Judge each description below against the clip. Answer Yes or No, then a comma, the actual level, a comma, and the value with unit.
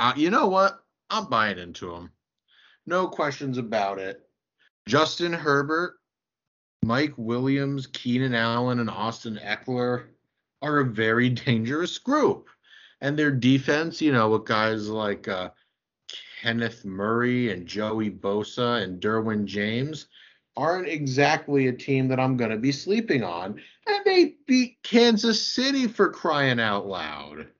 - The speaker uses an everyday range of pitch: No, wide, 5.9 semitones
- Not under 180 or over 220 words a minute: No, slow, 135 wpm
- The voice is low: Yes, low, 130 Hz